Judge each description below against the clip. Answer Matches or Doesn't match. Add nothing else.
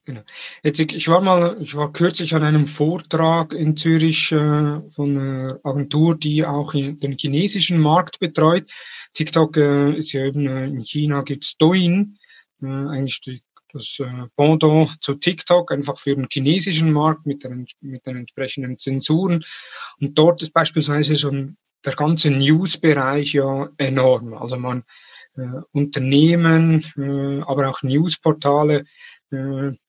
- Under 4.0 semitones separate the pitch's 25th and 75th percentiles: Matches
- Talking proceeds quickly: Doesn't match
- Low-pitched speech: Doesn't match